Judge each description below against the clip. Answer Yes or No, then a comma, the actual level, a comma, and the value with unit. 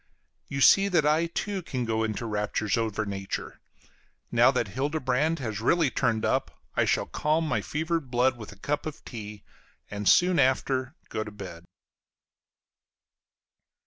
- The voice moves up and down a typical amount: No, wide, 6.2 semitones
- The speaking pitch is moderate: No, low, 130 Hz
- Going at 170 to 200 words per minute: No, average, 150 wpm